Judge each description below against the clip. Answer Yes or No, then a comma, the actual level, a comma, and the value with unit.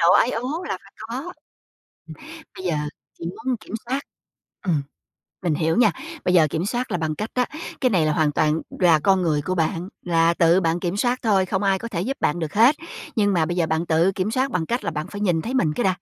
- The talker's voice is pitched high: No, medium, 180 Hz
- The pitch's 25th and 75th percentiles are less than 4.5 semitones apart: No, wide, 5.5 semitones